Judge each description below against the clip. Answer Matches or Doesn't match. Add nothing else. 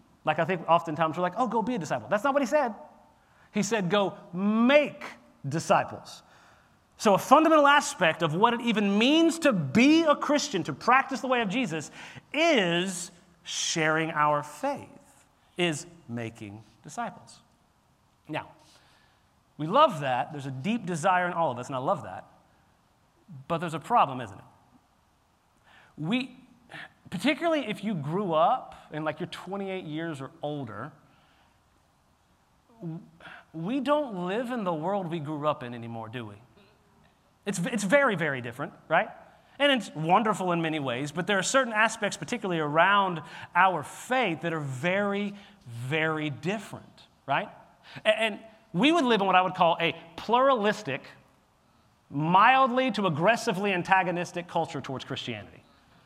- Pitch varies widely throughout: Matches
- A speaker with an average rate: Matches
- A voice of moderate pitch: Matches